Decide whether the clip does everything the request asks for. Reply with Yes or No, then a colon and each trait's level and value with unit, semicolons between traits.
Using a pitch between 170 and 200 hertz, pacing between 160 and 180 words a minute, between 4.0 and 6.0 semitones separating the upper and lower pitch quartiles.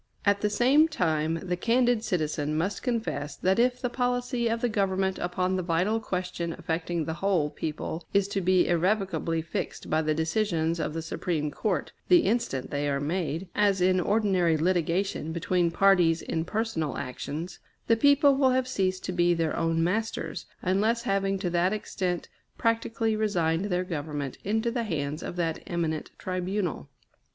Yes: medium, 185 Hz; average, 165 wpm; average, 4.7 semitones